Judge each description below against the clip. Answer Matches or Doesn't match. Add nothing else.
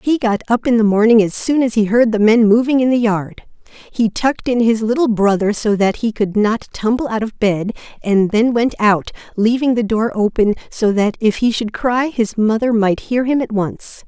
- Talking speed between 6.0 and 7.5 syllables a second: Doesn't match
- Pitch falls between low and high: Doesn't match